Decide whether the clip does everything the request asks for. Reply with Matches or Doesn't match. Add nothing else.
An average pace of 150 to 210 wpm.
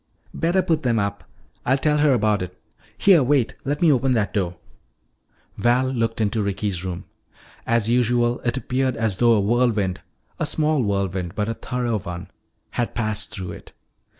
Matches